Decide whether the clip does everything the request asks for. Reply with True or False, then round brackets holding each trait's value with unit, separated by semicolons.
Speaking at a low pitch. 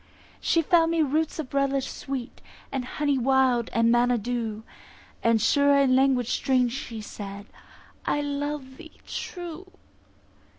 False (265 Hz)